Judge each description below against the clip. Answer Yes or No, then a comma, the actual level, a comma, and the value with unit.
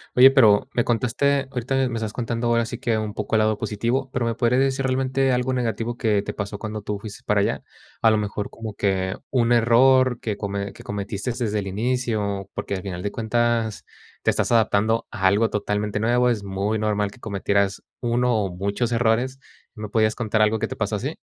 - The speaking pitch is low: Yes, low, 110 Hz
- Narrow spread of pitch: No, average, 3.0 semitones